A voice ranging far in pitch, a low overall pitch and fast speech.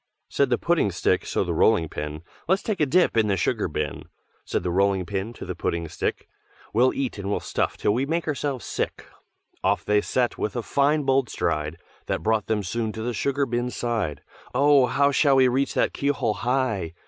Yes: wide, 5.8 semitones; low, 120 Hz; fast, 210 wpm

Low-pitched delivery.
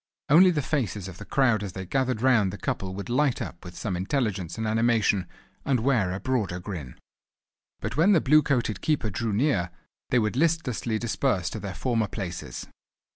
Yes: low, 110 Hz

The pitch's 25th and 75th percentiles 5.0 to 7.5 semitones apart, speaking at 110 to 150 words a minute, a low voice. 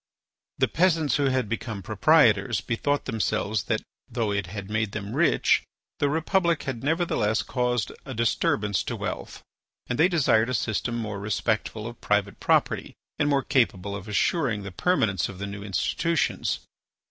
No: wide, 5.4 semitones; average, 160 wpm; low, 115 Hz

